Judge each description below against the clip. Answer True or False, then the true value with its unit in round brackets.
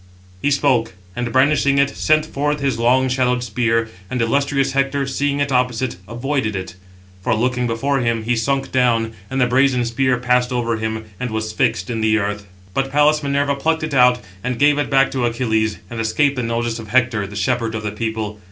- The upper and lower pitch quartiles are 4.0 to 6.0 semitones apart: False (3.3 semitones)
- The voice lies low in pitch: True (125 Hz)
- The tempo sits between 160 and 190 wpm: False (200 wpm)